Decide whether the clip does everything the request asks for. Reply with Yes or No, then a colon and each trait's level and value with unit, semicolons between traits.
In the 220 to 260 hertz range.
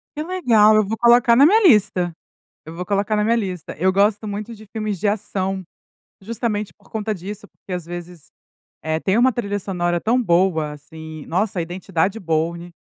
No: high, 200 Hz